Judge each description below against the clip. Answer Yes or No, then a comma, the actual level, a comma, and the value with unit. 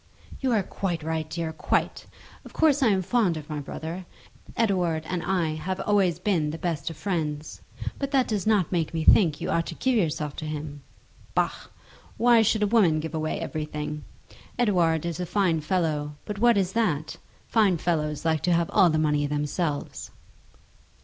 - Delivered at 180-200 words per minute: Yes, average, 185 wpm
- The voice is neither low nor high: Yes, medium, 170 Hz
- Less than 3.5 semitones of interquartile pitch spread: No, average, 4.3 semitones